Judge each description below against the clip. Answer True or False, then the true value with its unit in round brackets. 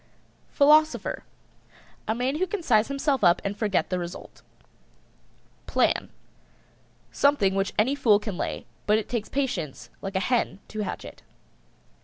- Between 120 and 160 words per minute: True (145 wpm)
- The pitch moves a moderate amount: False (6.1 semitones)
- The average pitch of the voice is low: False (215 Hz)